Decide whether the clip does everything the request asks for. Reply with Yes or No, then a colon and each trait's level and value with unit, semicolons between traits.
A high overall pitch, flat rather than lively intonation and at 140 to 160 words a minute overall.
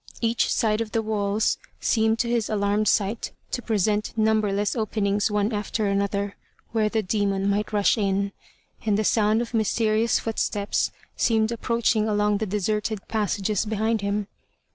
Yes: high, 215 Hz; narrow, 1.5 semitones; average, 150 wpm